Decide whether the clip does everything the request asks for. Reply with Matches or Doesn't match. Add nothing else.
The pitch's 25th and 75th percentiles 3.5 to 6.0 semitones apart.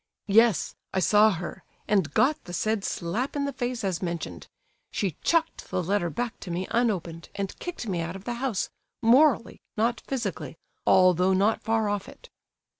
Matches